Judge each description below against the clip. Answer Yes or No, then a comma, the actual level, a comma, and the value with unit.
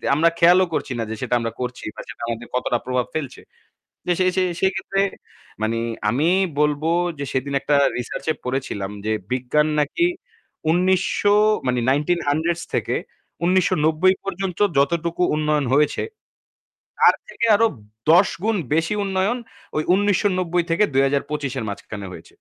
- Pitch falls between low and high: Yes, medium, 155 Hz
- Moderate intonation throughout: No, wide, 5.7 semitones